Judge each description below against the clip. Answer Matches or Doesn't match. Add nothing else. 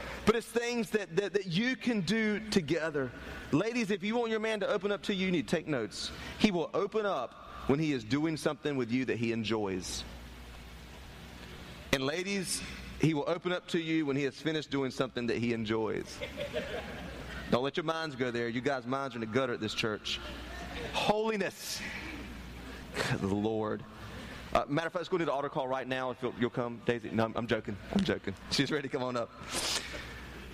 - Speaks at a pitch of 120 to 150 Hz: Matches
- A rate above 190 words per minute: Matches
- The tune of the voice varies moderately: Doesn't match